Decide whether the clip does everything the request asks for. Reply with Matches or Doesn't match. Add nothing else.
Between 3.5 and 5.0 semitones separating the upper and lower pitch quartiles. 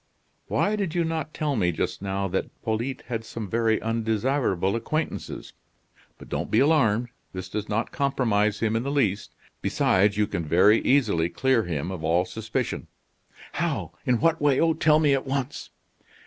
Doesn't match